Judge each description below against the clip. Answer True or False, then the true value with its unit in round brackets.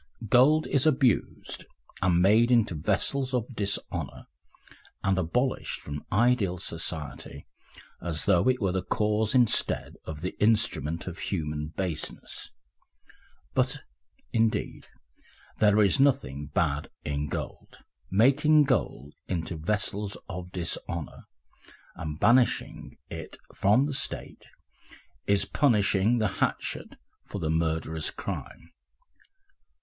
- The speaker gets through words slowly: True (110 wpm)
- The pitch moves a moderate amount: False (6.7 semitones)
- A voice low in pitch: True (100 Hz)